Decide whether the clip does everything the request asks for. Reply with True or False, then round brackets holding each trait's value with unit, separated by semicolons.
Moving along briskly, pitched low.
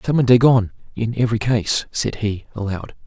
False (155 wpm; 115 Hz)